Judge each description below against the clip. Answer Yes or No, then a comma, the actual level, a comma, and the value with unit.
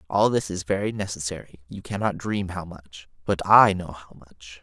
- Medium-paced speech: Yes, average, 195 wpm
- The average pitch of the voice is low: Yes, very low, 90 Hz